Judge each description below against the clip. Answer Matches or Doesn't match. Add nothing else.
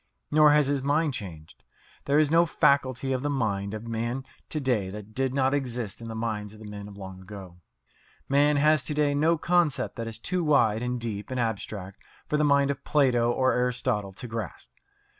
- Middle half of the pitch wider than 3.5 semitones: Matches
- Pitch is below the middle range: Matches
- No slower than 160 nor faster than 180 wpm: Doesn't match